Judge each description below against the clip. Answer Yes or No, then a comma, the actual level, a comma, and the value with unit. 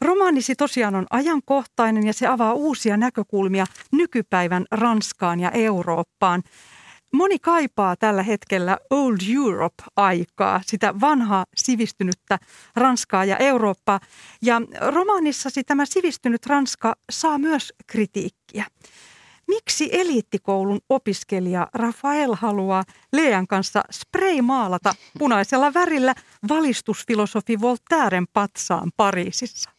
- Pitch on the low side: No, high, 230 Hz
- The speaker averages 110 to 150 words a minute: No, slow, 95 wpm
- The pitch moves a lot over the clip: Yes, wide, 5.9 semitones